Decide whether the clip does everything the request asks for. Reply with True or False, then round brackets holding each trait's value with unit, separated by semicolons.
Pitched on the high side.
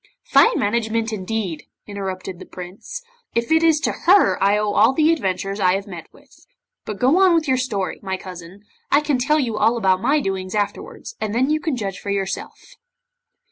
True (215 Hz)